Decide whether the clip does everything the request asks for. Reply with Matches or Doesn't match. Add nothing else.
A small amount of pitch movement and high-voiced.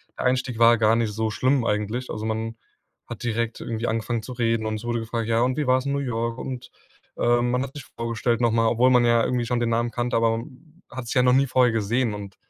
Doesn't match